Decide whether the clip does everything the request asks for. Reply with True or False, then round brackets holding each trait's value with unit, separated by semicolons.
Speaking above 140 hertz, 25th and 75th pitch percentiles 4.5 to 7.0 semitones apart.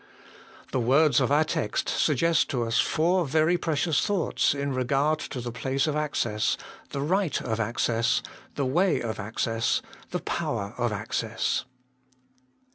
False (135 Hz; 5.1 semitones)